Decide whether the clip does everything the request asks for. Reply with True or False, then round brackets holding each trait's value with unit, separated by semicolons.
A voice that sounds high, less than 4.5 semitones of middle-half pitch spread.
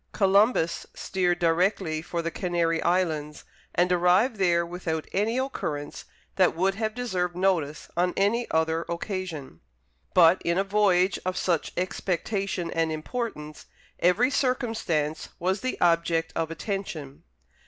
False (180 Hz; 3.1 semitones)